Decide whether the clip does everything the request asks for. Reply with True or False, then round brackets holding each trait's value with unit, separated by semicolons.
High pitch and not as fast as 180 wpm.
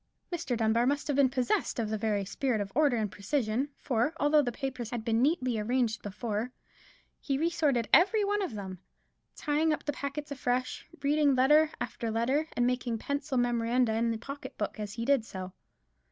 False (250 Hz; 190 wpm)